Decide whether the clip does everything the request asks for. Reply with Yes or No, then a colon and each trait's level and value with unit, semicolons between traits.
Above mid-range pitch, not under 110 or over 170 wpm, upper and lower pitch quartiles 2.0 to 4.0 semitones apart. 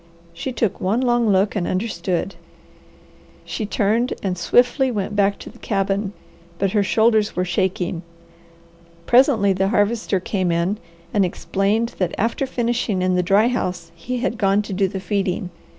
Yes: high, 200 Hz; average, 160 wpm; average, 3.5 semitones